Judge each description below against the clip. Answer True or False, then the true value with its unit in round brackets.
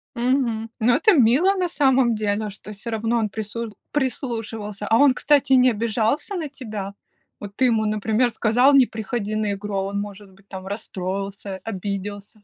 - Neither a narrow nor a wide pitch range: True (3.5 semitones)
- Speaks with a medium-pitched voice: False (220 Hz)